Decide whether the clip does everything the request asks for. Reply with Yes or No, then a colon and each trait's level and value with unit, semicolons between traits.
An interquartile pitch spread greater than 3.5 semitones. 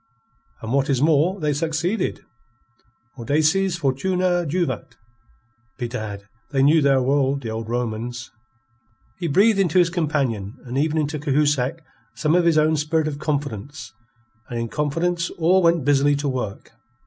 Yes: average, 4.1 semitones